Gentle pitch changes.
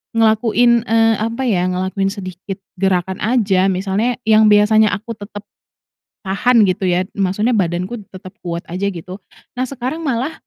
No: average, 3.3 semitones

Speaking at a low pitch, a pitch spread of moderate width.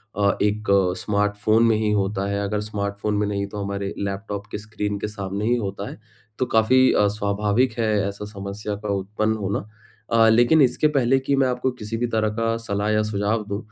No: low, 105 Hz; narrow, 1.8 semitones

